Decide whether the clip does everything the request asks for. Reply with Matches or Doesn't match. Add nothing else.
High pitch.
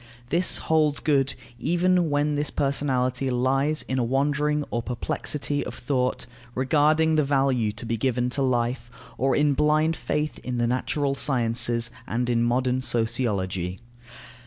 Doesn't match